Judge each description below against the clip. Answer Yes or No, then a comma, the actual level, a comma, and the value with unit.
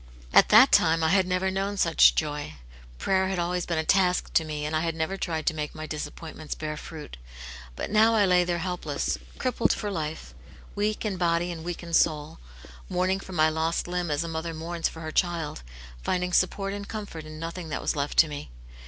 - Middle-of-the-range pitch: Yes, medium, 170 Hz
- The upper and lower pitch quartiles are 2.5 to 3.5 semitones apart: Yes, average, 2.9 semitones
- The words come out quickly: Yes, fast, 215 wpm